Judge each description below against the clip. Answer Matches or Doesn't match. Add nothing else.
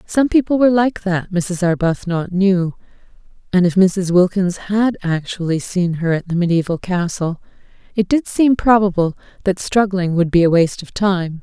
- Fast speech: Doesn't match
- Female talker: Matches